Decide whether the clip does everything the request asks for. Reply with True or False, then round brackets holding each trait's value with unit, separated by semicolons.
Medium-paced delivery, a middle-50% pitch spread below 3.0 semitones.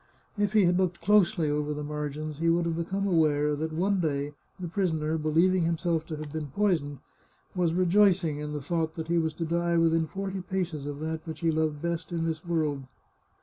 False (215 wpm; 2.5 semitones)